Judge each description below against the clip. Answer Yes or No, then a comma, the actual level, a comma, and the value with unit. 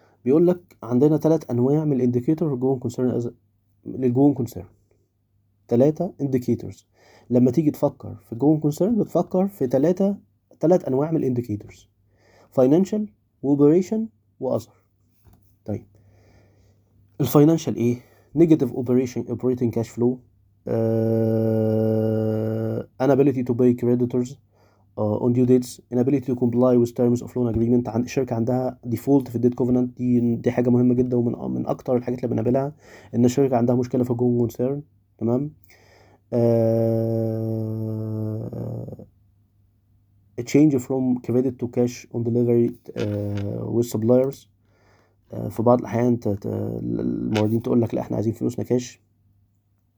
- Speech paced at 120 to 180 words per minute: Yes, average, 125 wpm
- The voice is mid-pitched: No, low, 120 Hz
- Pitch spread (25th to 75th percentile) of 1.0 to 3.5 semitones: Yes, average, 3.2 semitones